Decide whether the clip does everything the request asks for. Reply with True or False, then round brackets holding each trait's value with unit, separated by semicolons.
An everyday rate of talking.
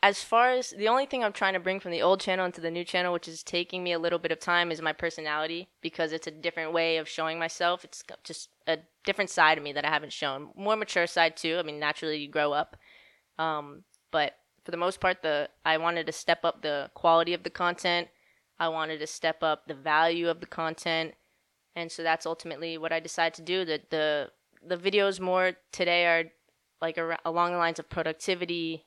False (225 wpm)